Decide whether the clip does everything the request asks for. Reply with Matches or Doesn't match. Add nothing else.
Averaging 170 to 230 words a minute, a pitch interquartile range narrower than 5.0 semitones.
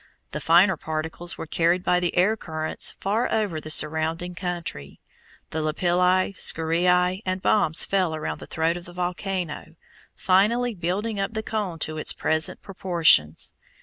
Doesn't match